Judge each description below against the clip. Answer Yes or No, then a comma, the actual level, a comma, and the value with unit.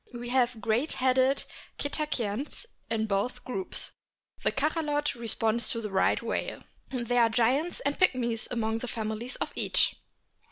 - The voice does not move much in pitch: No, average, 3.3 semitones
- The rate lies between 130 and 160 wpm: Yes, average, 145 wpm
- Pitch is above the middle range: Yes, high, 245 Hz